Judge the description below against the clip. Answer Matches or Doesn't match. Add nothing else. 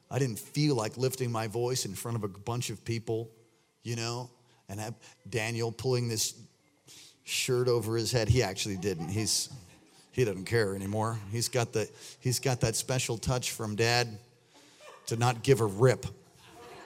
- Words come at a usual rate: Matches